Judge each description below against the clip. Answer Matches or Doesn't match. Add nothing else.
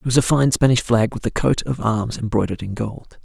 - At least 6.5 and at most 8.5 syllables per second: Doesn't match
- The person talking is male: Matches